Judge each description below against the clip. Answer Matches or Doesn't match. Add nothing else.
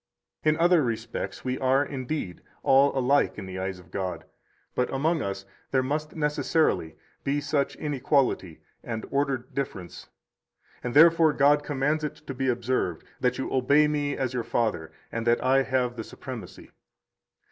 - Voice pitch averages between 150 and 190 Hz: Doesn't match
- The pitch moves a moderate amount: Matches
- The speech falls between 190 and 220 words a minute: Doesn't match